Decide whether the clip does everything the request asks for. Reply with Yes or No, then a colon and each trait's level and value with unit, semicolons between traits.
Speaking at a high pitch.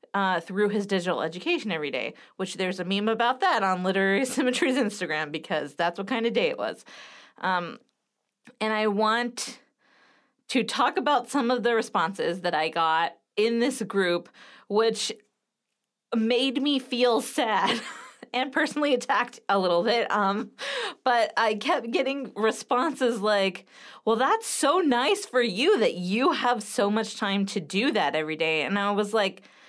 Yes: high, 220 Hz